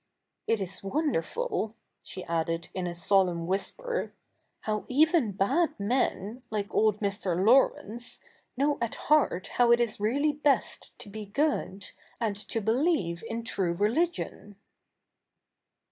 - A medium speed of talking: No, slow, 130 wpm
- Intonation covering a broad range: Yes, wide, 5.7 semitones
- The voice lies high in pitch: Yes, high, 215 Hz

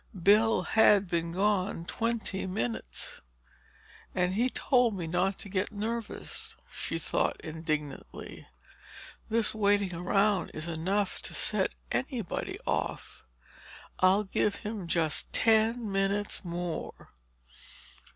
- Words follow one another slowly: Yes, slow, 105 wpm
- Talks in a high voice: Yes, high, 195 Hz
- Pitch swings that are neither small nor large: Yes, average, 3.6 semitones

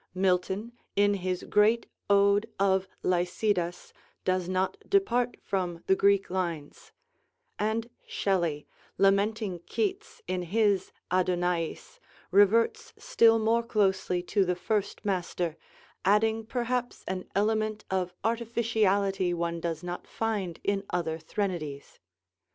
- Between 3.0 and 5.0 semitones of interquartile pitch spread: Yes, average, 3.5 semitones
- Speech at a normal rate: No, slow, 110 wpm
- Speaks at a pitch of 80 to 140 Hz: No, high, 195 Hz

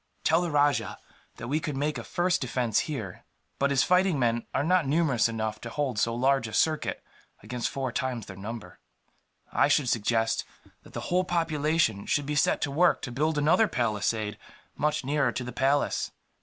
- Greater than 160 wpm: Yes, average, 185 wpm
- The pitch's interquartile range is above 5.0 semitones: No, average, 4.7 semitones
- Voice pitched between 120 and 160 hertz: Yes, low, 135 Hz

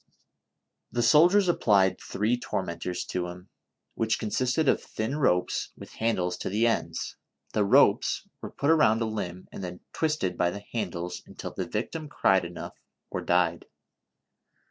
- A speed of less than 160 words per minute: Yes, average, 150 wpm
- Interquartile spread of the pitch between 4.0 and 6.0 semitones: Yes, average, 5.2 semitones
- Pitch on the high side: No, low, 105 Hz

